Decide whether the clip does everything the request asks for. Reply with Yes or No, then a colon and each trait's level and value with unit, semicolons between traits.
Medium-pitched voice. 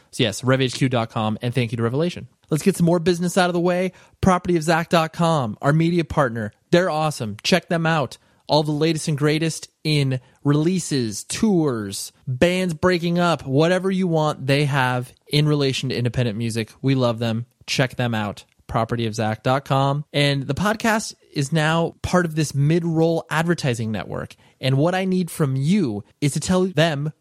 Yes: medium, 150 Hz